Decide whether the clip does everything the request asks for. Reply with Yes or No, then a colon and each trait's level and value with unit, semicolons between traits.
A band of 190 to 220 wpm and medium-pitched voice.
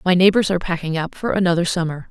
No: fast, 230 wpm; medium, 175 Hz